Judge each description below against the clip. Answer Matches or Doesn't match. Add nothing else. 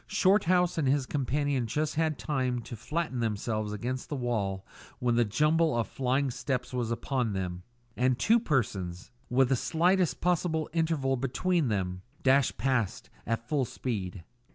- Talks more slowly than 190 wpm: Matches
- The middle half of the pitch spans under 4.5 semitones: Doesn't match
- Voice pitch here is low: Matches